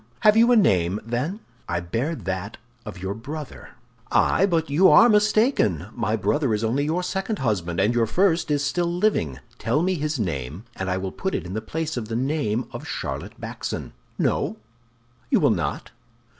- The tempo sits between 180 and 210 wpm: Yes, average, 185 wpm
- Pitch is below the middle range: Yes, low, 130 Hz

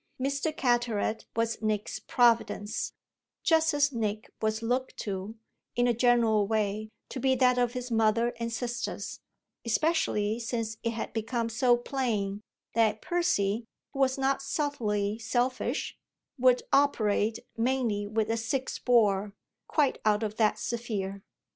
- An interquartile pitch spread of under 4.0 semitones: Yes, average, 2.9 semitones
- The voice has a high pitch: Yes, high, 230 Hz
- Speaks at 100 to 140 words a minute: Yes, slow, 135 wpm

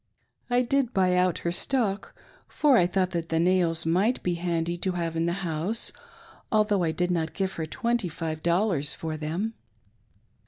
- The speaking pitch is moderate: Yes, medium, 180 Hz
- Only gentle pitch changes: No, average, 3.5 semitones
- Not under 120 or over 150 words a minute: No, average, 170 wpm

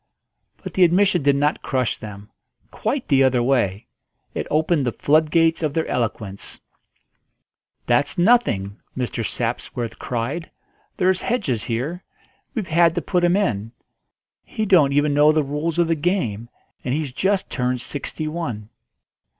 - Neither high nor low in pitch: Yes, medium, 145 Hz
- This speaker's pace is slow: No, average, 145 wpm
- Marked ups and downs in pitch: Yes, wide, 6.0 semitones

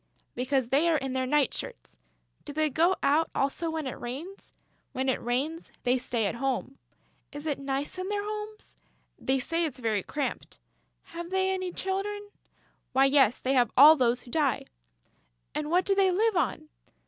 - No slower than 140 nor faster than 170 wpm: No, average, 185 wpm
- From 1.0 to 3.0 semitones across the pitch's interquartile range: No, wide, 5.4 semitones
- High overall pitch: Yes, very high, 290 Hz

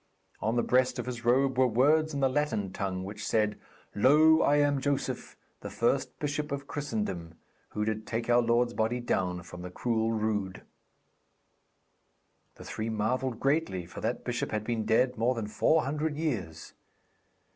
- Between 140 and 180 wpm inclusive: Yes, average, 165 wpm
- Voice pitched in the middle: No, low, 120 Hz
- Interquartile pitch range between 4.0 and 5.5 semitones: Yes, average, 4.5 semitones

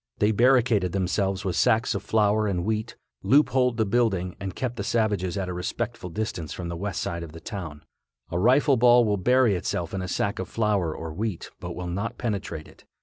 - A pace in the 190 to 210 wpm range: Yes, fast, 205 wpm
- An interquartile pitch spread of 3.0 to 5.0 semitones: Yes, average, 4.3 semitones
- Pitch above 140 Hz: No, low, 100 Hz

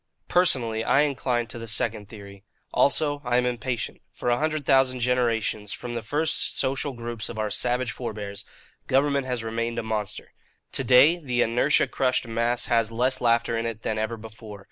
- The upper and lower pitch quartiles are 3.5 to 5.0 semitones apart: No, narrow, 2.5 semitones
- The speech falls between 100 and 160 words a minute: No, average, 180 wpm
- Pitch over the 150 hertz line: No, low, 120 Hz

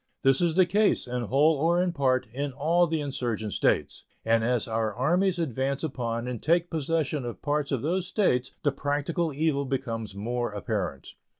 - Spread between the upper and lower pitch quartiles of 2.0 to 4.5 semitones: No, average, 5.0 semitones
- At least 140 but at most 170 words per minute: No, average, 180 wpm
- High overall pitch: No, medium, 140 Hz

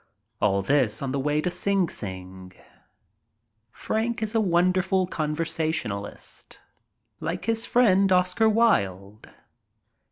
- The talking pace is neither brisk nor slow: No, slow, 105 wpm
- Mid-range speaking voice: Yes, medium, 165 Hz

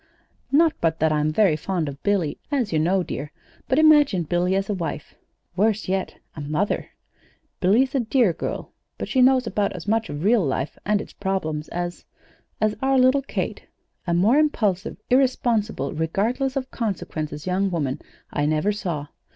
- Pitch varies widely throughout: Yes, wide, 6.8 semitones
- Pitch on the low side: No, high, 195 Hz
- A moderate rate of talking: Yes, average, 170 wpm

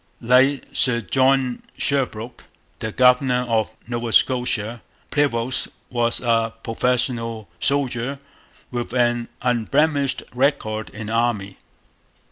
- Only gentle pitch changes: Yes, narrow, 2.2 semitones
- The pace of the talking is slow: Yes, slow, 100 wpm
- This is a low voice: Yes, low, 120 Hz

